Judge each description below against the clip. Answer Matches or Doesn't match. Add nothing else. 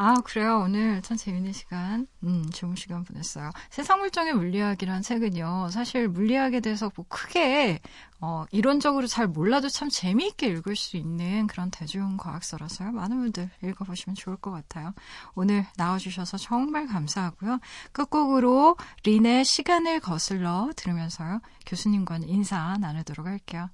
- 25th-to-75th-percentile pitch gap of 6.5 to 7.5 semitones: Doesn't match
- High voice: Matches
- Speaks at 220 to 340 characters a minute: Doesn't match